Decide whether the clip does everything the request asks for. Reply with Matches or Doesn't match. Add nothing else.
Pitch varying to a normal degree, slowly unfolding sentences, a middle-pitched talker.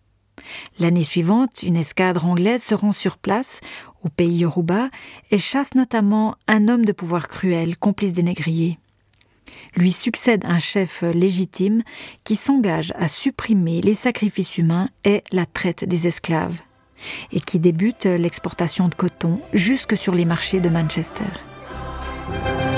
Matches